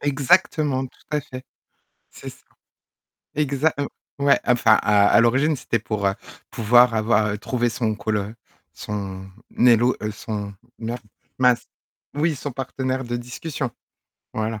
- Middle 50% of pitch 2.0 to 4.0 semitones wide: Yes, average, 3.7 semitones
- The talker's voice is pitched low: Yes, low, 120 Hz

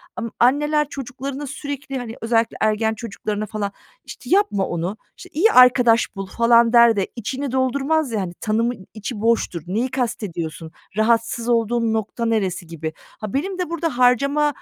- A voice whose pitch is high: Yes, high, 235 Hz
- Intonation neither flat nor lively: Yes, average, 3.9 semitones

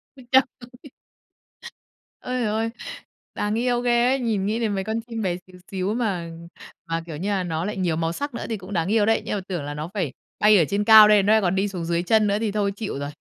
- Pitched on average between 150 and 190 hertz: No, high, 205 Hz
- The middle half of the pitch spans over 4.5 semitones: No, average, 3.9 semitones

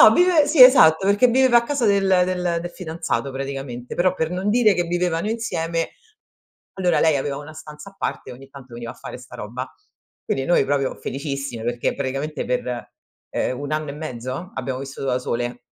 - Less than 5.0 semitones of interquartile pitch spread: No, wide, 5.7 semitones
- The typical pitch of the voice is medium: Yes, medium, 155 Hz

